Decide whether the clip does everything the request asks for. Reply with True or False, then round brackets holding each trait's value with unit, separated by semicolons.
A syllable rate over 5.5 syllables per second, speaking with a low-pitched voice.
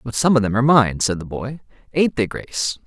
True (5.9 syllables/s; 120 Hz)